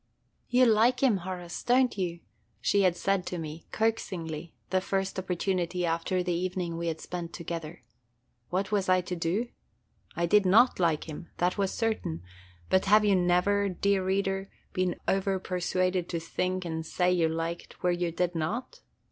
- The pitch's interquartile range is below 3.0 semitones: Yes, narrow, 2.5 semitones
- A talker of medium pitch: Yes, medium, 180 Hz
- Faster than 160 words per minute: Yes, average, 170 wpm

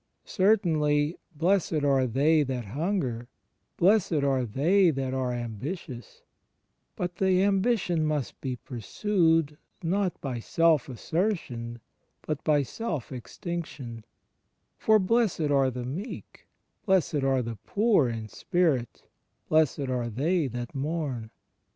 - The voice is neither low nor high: Yes, medium, 150 Hz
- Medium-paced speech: No, slow, 115 wpm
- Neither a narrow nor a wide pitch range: No, wide, 5.8 semitones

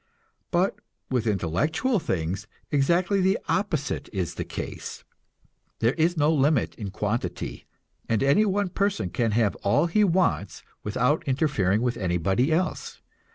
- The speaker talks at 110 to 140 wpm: Yes, slow, 135 wpm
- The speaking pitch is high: No, low, 135 Hz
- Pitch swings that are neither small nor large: No, wide, 9.0 semitones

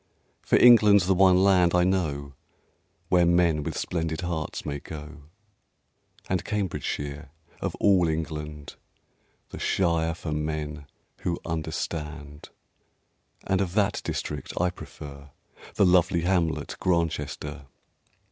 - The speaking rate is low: Yes, slow, 115 wpm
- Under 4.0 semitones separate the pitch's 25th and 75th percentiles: Yes, average, 3.3 semitones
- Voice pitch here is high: No, very low, 80 Hz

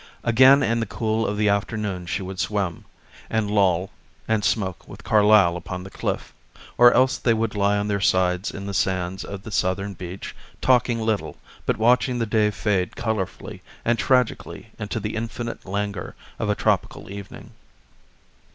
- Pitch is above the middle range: No, low, 105 Hz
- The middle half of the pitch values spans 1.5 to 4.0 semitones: Yes, average, 2.8 semitones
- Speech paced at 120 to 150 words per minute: No, average, 170 wpm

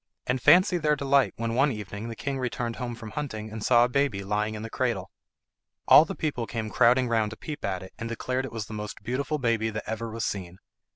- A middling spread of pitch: Yes, average, 3.5 semitones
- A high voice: No, low, 115 Hz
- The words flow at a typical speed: No, fast, 235 wpm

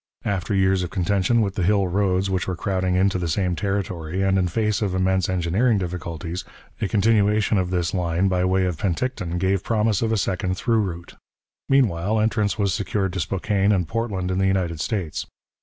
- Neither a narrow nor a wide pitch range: No, narrow, 2.2 semitones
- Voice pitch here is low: Yes, very low, 95 Hz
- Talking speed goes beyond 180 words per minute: Yes, average, 190 wpm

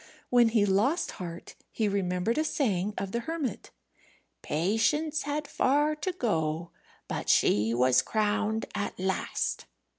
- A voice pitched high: Yes, high, 215 Hz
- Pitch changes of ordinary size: No, wide, 7.5 semitones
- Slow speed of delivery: Yes, slow, 130 wpm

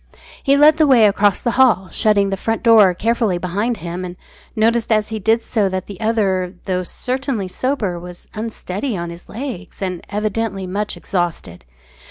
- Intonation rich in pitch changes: No, average, 3.8 semitones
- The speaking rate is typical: Yes, average, 175 wpm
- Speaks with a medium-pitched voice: No, high, 210 Hz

